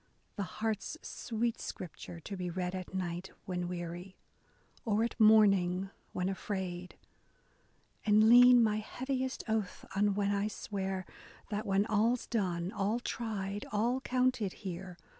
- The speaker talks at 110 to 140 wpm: Yes, slow, 135 wpm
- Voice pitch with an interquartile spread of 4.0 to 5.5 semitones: No, average, 3.1 semitones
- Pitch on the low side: No, high, 205 Hz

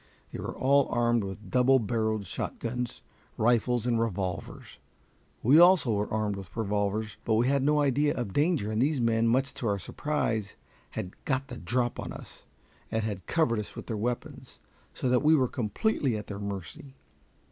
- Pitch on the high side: No, low, 115 Hz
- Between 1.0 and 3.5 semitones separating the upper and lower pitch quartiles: No, average, 3.9 semitones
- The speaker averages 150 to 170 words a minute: No, average, 180 wpm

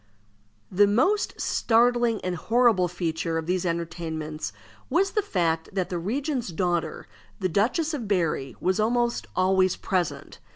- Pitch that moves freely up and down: Yes, wide, 5.8 semitones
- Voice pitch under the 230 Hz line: Yes, medium, 185 Hz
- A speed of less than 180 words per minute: Yes, slow, 135 wpm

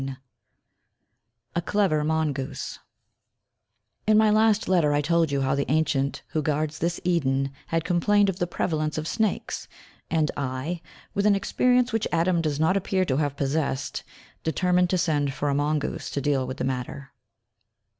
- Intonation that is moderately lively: Yes, average, 4.2 semitones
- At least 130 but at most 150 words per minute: No, average, 165 wpm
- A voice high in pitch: No, medium, 155 Hz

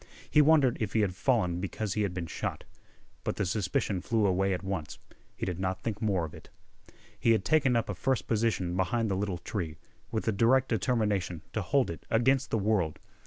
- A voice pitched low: Yes, low, 105 Hz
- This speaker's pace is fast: Yes, fast, 210 wpm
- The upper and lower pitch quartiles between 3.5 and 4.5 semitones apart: Yes, average, 3.9 semitones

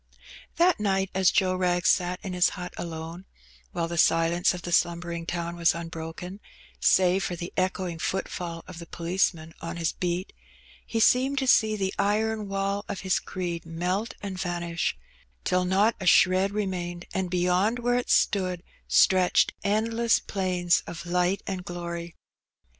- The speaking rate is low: No, average, 160 wpm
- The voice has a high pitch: No, medium, 180 Hz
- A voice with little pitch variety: Yes, narrow, 2.3 semitones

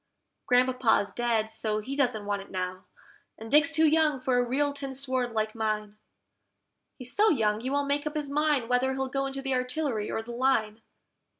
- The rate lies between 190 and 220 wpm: Yes, average, 195 wpm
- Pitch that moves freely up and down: No, average, 4.1 semitones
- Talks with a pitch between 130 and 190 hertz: No, very high, 255 Hz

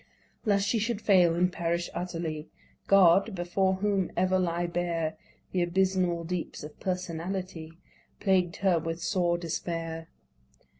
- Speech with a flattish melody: Yes, narrow, 2.0 semitones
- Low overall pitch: No, medium, 175 Hz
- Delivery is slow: Yes, slow, 130 wpm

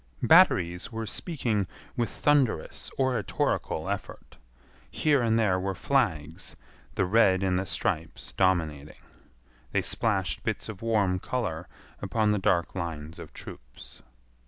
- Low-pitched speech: Yes, very low, 95 Hz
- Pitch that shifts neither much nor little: Yes, average, 4.8 semitones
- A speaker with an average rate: No, slow, 125 wpm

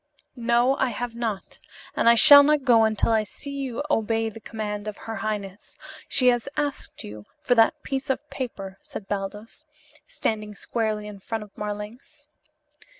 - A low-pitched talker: No, high, 225 Hz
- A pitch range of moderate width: Yes, average, 3.5 semitones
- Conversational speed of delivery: Yes, average, 165 wpm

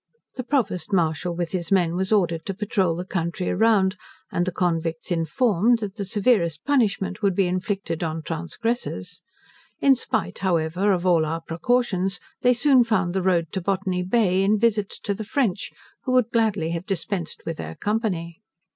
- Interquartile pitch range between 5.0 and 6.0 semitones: No, average, 4.1 semitones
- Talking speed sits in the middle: Yes, average, 175 wpm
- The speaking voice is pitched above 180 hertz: Yes, high, 190 Hz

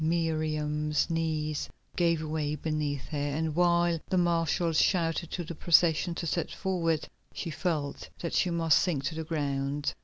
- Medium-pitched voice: Yes, medium, 160 Hz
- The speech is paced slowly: No, average, 155 wpm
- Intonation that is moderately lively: No, narrow, 2.0 semitones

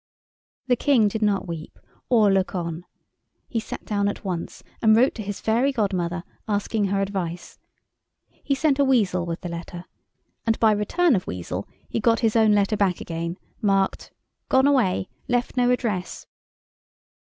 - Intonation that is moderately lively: Yes, average, 4.2 semitones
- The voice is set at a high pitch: Yes, high, 205 Hz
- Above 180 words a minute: No, average, 165 wpm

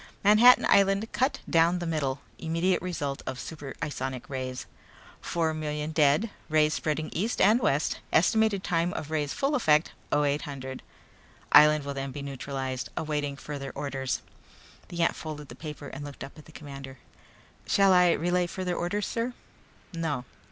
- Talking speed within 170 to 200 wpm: No, average, 155 wpm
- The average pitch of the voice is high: No, medium, 155 Hz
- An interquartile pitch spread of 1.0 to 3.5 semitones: No, average, 4.1 semitones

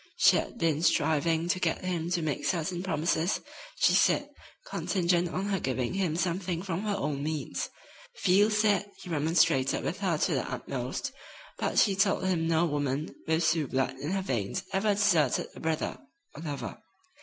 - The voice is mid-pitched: Yes, medium, 170 Hz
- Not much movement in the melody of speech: No, average, 3.4 semitones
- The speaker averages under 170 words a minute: No, average, 175 wpm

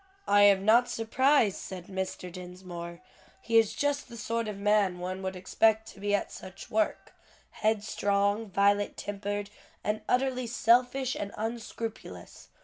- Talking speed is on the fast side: No, average, 140 wpm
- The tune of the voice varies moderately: Yes, average, 3.0 semitones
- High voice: Yes, high, 205 Hz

